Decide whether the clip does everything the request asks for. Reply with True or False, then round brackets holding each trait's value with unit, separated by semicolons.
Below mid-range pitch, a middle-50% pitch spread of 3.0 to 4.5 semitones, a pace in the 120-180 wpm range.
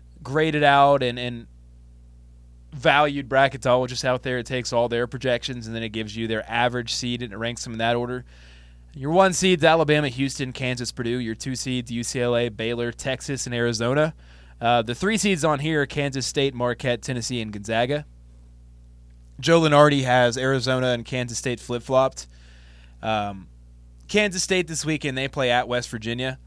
True (125 Hz; 3.3 semitones; 175 wpm)